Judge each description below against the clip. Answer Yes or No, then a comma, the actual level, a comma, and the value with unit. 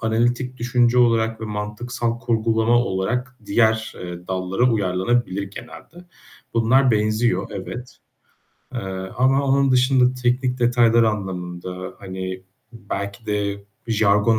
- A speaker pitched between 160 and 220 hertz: No, low, 115 Hz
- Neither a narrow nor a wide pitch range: Yes, average, 3.4 semitones